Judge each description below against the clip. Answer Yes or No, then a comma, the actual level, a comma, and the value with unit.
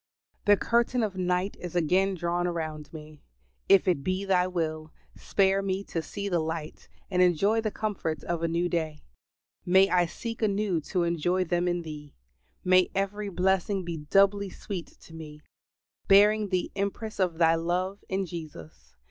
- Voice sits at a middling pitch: Yes, medium, 180 Hz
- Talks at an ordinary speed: Yes, average, 165 wpm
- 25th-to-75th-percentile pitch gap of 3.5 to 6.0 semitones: No, average, 3.0 semitones